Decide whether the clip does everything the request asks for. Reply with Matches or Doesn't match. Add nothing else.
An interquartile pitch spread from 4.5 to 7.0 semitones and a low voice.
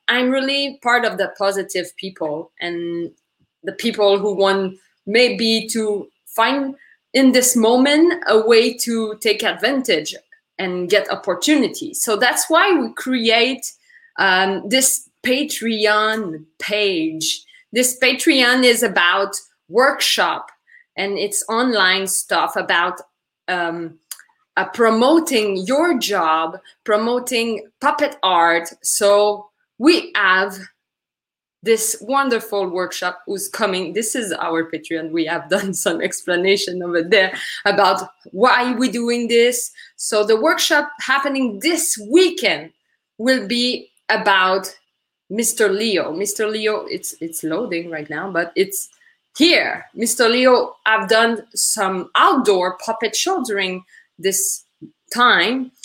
Doesn't match